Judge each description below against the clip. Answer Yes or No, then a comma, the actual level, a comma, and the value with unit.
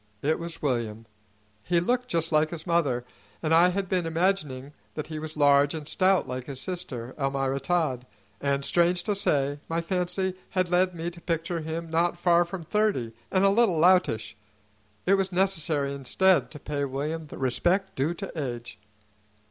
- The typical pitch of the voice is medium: Yes, medium, 165 Hz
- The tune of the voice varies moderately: Yes, average, 4.3 semitones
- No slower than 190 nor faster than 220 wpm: No, average, 175 wpm